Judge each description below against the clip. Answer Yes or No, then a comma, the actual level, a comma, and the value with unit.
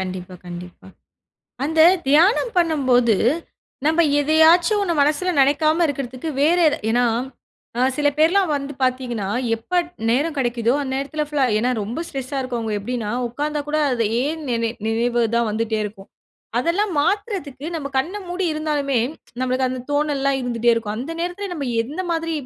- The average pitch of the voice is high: Yes, very high, 280 Hz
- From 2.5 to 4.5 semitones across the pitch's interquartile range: No, average, 5.0 semitones